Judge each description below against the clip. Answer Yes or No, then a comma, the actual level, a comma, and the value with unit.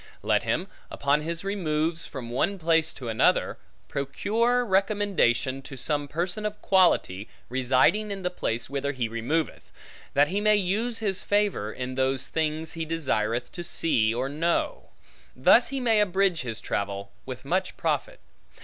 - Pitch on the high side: No, medium, 160 Hz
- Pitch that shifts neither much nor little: No, wide, 7.1 semitones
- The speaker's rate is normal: Yes, average, 155 wpm